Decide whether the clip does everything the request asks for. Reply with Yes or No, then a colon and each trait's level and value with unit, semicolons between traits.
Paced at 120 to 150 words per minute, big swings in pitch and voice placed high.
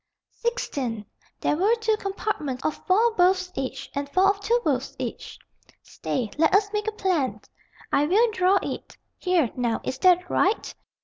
No: average, 165 wpm; wide, 6.9 semitones; very high, 370 Hz